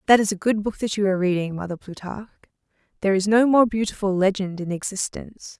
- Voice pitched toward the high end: Yes, high, 200 Hz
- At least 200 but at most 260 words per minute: Yes, fast, 205 wpm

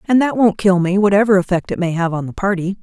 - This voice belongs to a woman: Yes, female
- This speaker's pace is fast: Yes, fast, 275 wpm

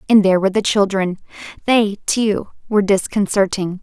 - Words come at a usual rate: No, slow, 125 wpm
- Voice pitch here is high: Yes, high, 200 Hz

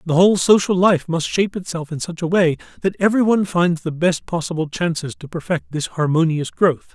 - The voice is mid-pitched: Yes, medium, 170 Hz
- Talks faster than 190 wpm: Yes, average, 200 wpm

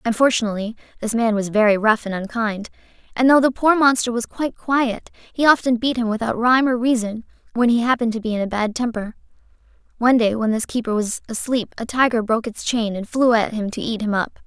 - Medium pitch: No, high, 230 Hz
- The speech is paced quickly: Yes, fast, 220 wpm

